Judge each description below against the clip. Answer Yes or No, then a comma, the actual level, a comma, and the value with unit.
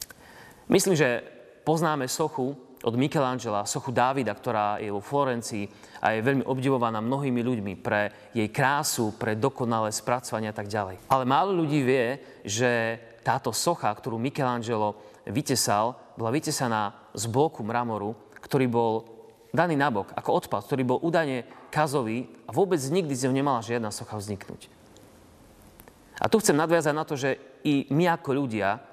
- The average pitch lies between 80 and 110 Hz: No, low, 125 Hz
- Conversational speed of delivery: Yes, average, 150 wpm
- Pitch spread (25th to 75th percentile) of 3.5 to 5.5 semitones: Yes, average, 4.3 semitones